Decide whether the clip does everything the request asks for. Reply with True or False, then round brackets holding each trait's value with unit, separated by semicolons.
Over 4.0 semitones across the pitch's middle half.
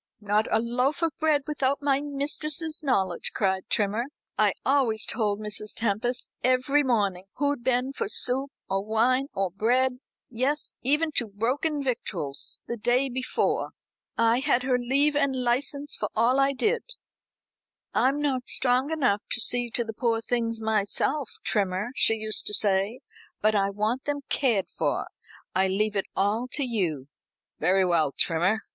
True (4.6 semitones)